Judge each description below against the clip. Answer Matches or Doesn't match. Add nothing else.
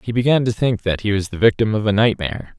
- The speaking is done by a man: Matches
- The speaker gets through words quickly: Matches